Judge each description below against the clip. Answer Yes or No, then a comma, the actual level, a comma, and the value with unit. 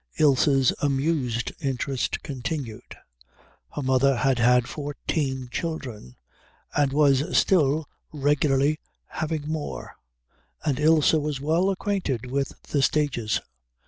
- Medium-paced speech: No, slow, 105 wpm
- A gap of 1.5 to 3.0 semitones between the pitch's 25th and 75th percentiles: Yes, average, 2.7 semitones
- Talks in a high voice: No, medium, 140 Hz